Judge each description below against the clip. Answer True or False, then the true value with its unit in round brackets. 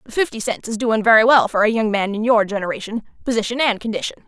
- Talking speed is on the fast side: True (240 wpm)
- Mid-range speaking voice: False (220 Hz)